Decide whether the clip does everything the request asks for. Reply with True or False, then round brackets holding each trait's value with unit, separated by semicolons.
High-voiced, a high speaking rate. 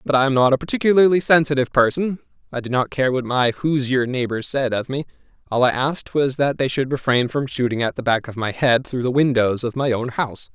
False (130 Hz; 240 wpm)